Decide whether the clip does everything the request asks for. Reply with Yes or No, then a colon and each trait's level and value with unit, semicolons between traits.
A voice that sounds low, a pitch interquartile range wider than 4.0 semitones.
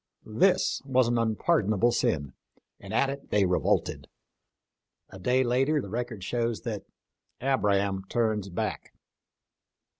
Yes: low, 115 Hz; average, 4.4 semitones